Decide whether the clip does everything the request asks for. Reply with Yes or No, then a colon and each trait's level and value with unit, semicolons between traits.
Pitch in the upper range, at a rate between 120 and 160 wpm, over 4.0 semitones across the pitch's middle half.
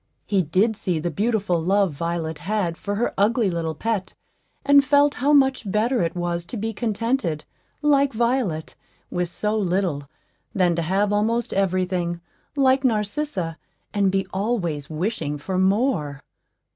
Yes: high, 195 Hz; average, 150 wpm; average, 5.1 semitones